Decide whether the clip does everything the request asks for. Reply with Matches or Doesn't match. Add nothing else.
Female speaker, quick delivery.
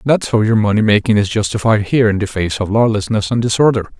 Doesn't match